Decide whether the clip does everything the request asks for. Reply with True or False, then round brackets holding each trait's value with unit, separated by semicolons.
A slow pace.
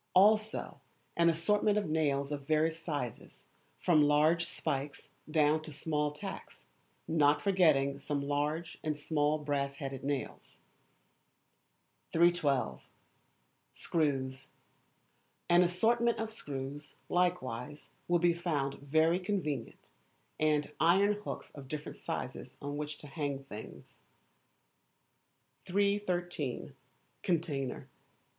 True (105 wpm)